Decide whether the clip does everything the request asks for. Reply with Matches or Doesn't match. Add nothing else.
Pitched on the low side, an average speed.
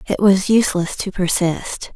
Doesn't match